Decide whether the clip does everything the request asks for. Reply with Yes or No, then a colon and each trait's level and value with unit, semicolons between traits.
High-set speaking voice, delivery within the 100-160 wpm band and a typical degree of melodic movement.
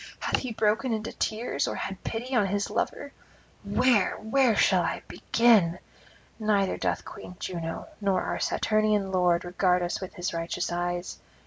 Yes: high, 200 Hz; average, 155 wpm; average, 3.8 semitones